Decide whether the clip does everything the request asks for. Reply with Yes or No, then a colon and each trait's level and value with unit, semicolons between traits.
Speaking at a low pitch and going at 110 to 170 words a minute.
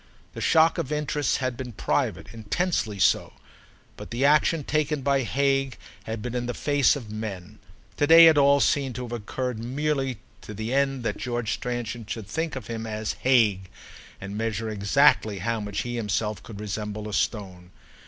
No: low, 120 Hz; average, 180 wpm